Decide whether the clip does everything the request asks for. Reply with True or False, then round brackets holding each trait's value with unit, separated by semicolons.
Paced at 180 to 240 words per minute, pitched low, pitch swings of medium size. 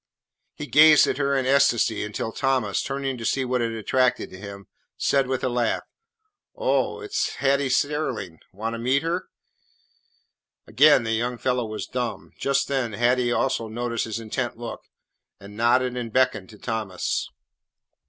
False (160 wpm; 125 Hz; 3.2 semitones)